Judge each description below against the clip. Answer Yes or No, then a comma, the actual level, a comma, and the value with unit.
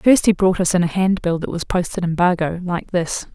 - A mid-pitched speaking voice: Yes, medium, 180 Hz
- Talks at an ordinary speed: No, fast, 250 wpm